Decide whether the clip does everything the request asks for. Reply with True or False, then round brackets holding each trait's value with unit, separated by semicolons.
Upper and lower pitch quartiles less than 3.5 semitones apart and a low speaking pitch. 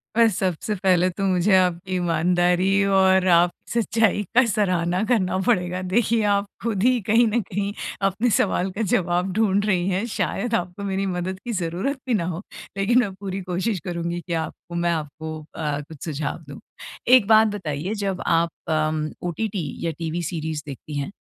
False (3.1 semitones; 185 Hz)